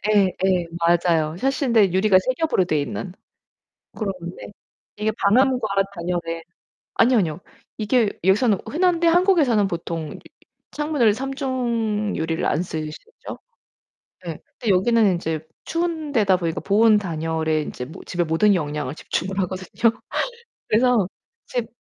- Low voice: No, high, 200 Hz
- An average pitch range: No, wide, 6.2 semitones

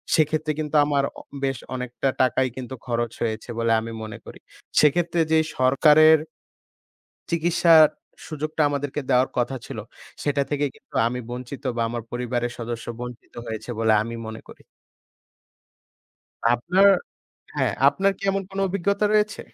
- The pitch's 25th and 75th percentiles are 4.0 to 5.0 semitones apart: Yes, average, 4.6 semitones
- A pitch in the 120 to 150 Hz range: Yes, medium, 140 Hz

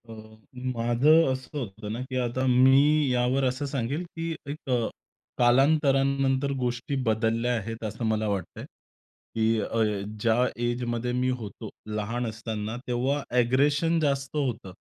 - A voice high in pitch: No, low, 125 Hz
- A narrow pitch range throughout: No, average, 3.2 semitones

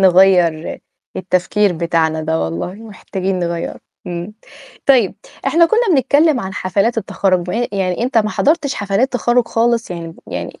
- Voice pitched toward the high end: Yes, high, 195 Hz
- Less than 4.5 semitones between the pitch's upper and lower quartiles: No, average, 5.3 semitones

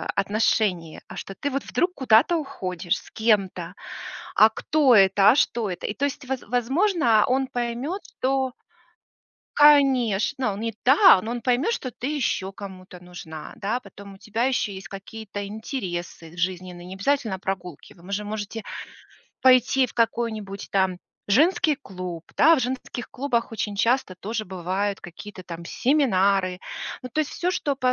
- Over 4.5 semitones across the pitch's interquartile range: Yes, wide, 5.5 semitones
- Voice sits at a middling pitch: No, high, 220 Hz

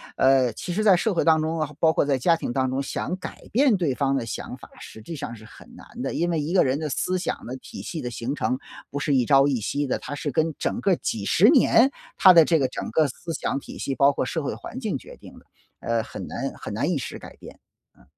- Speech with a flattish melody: No, average, 4.8 semitones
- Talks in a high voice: No, medium, 145 Hz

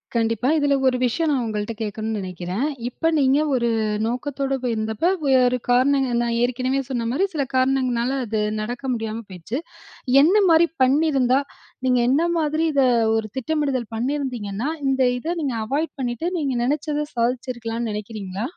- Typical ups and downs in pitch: Yes, average, 3.4 semitones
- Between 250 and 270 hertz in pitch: Yes, very high, 255 Hz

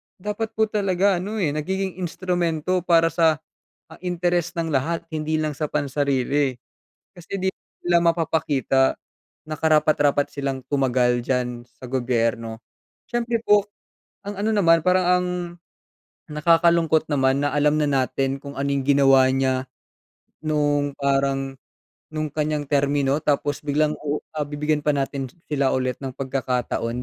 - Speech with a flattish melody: No, average, 3.7 semitones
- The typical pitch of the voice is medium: Yes, medium, 150 Hz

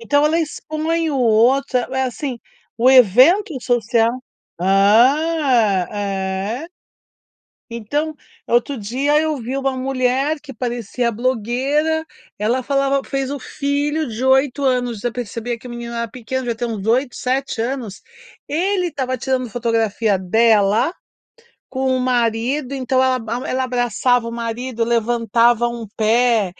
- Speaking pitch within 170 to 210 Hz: No, high, 245 Hz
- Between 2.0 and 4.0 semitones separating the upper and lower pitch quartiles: Yes, average, 3.0 semitones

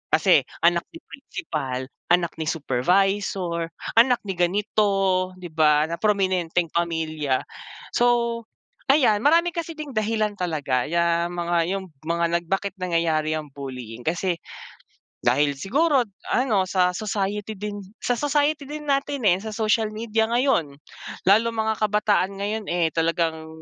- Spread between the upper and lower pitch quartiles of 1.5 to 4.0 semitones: No, average, 4.8 semitones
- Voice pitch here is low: No, high, 190 Hz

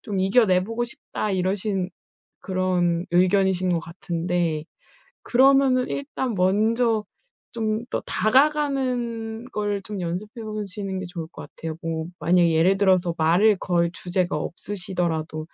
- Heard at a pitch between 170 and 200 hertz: Yes, high, 190 Hz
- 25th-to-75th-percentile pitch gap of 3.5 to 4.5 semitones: Yes, average, 4.0 semitones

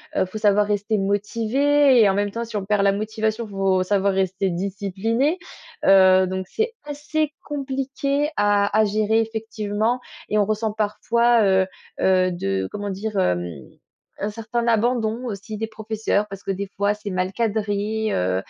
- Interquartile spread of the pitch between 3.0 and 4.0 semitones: No, narrow, 2.6 semitones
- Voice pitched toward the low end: No, high, 210 Hz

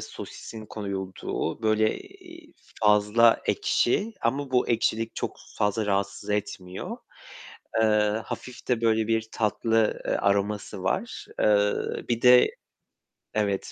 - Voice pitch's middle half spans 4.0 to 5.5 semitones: No, narrow, 2.5 semitones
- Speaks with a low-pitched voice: Yes, low, 110 Hz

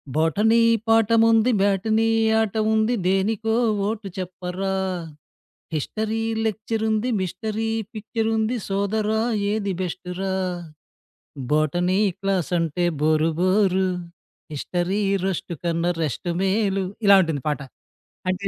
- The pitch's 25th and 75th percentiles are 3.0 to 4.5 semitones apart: Yes, average, 3.5 semitones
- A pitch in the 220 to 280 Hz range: No, high, 195 Hz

